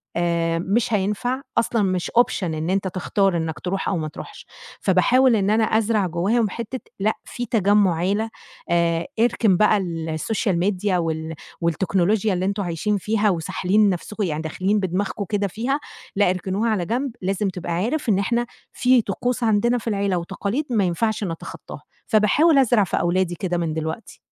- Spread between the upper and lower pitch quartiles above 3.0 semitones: Yes, average, 4.0 semitones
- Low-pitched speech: No, high, 195 Hz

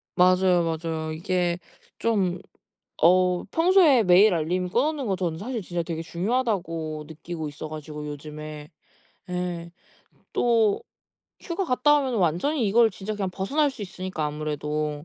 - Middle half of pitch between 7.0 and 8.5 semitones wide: No, wide, 5.6 semitones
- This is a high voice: No, medium, 180 Hz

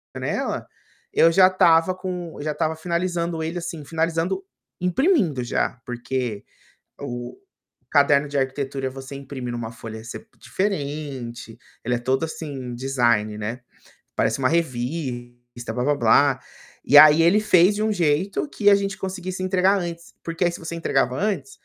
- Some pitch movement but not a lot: No, wide, 5.9 semitones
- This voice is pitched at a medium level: Yes, medium, 150 Hz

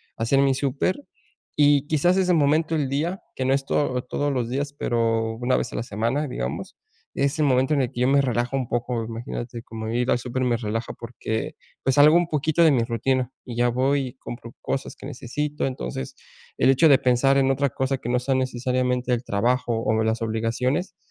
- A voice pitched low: Yes, low, 130 Hz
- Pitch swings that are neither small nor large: Yes, average, 3.0 semitones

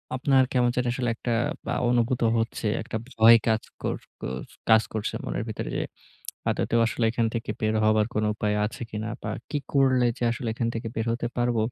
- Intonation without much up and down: Yes, narrow, 1.9 semitones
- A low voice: Yes, low, 115 Hz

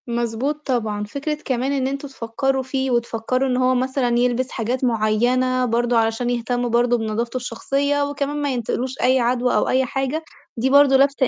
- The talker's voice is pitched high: Yes, very high, 255 Hz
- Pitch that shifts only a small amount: Yes, narrow, 2.2 semitones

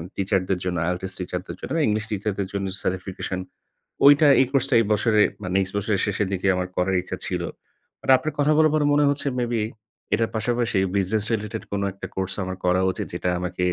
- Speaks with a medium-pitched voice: No, low, 100 Hz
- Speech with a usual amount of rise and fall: Yes, average, 4.0 semitones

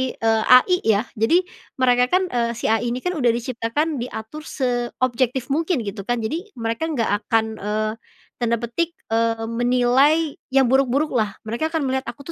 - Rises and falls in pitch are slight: No, average, 3.8 semitones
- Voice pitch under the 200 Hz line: No, high, 245 Hz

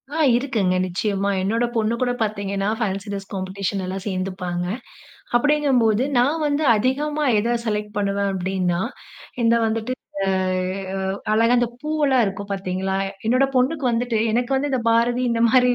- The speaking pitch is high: Yes, high, 220 Hz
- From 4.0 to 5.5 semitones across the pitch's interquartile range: Yes, average, 4.3 semitones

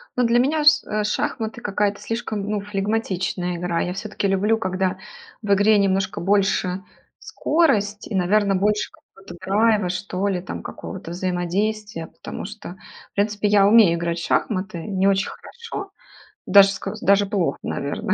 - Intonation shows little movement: Yes, narrow, 2.3 semitones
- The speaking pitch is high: Yes, high, 200 Hz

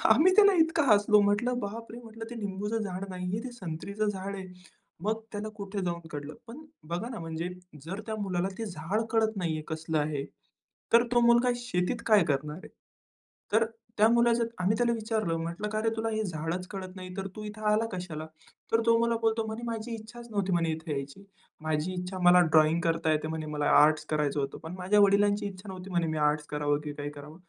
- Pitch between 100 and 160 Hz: No, high, 195 Hz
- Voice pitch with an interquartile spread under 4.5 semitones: No, wide, 5.4 semitones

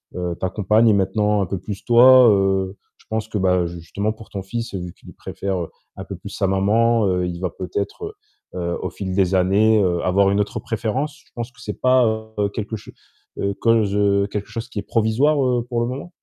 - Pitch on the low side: Yes, low, 105 Hz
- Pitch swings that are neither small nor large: Yes, average, 3.4 semitones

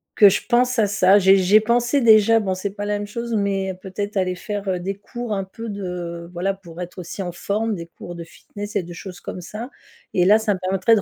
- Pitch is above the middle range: Yes, high, 200 Hz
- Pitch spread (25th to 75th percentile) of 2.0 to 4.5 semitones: Yes, average, 2.7 semitones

